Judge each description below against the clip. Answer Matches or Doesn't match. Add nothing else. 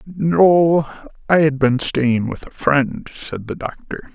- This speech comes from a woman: Doesn't match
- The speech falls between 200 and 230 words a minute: Doesn't match